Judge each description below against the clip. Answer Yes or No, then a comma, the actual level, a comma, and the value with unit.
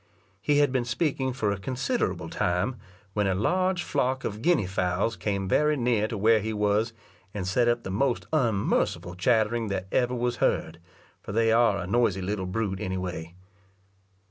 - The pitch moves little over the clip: No, average, 4.4 semitones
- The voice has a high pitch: No, low, 110 Hz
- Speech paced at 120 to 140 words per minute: No, average, 175 wpm